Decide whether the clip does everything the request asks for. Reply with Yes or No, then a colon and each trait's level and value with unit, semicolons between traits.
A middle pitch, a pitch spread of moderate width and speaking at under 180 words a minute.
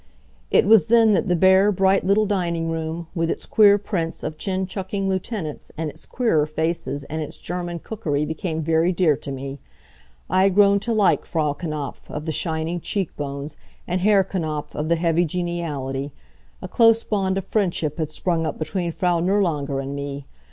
No: medium, 170 Hz; average, 3.9 semitones; average, 185 wpm